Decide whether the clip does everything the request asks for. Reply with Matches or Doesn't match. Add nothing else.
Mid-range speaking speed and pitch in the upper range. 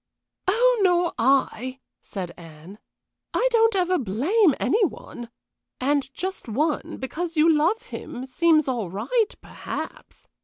Doesn't match